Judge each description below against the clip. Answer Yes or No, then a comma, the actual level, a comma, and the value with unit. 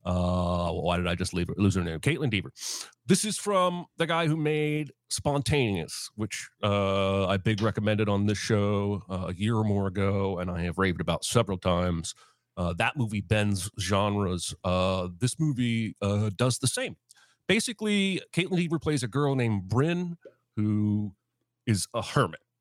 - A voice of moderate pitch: No, low, 105 Hz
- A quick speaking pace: No, average, 175 wpm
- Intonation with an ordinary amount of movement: No, wide, 5.9 semitones